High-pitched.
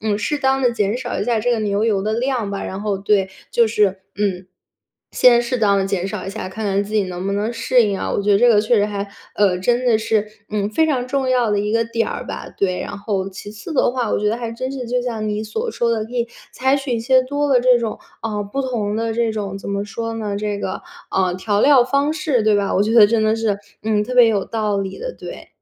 Yes: high, 220 Hz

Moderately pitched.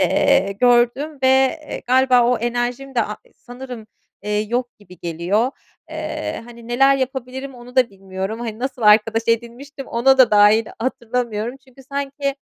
No: high, 240 Hz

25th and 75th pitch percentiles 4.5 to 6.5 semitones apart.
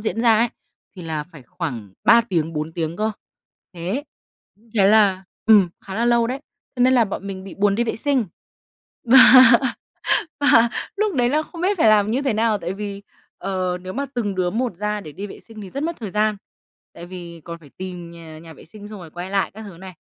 Yes: average, 4.8 semitones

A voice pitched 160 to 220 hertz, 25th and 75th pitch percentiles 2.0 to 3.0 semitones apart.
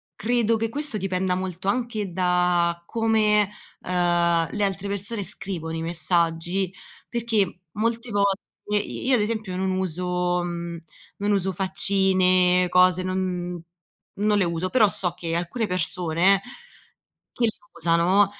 Yes: medium, 185 Hz; average, 2.7 semitones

